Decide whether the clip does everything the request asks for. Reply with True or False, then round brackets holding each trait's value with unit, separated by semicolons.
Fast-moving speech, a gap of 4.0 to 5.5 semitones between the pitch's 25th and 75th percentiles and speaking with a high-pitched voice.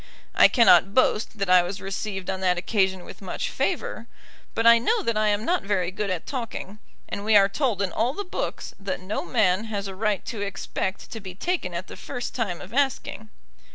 False (215 wpm; 3.4 semitones; 205 Hz)